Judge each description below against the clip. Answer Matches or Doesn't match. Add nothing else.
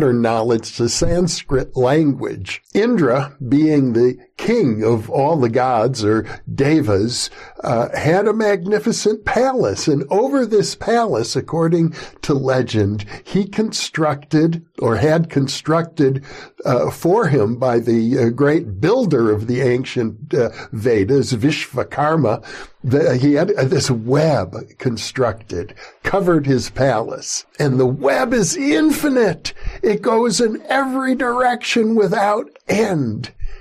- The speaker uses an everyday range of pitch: Doesn't match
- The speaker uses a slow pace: Matches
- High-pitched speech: Doesn't match